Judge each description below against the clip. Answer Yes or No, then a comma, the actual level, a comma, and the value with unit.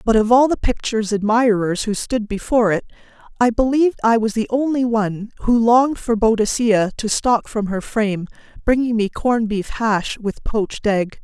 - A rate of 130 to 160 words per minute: No, average, 180 wpm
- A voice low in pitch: No, high, 225 Hz